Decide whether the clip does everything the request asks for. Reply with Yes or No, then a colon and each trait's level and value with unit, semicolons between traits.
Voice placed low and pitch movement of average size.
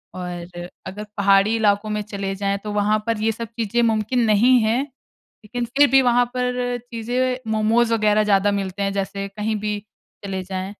No: high, 215 Hz; average, 3.0 semitones